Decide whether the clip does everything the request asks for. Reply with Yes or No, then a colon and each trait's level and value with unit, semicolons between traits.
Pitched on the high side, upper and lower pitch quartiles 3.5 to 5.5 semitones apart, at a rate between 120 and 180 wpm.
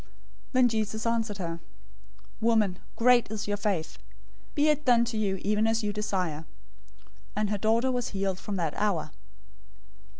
No: high, 210 Hz; average, 2.9 semitones; average, 160 wpm